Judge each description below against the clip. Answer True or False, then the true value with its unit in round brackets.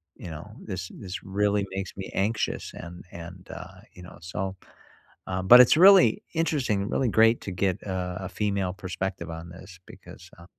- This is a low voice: True (95 Hz)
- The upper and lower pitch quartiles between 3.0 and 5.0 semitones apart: False (2.6 semitones)